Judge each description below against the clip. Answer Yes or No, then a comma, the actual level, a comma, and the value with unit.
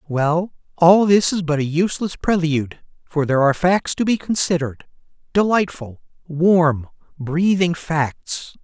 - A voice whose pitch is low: No, medium, 165 Hz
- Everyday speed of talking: No, slow, 125 wpm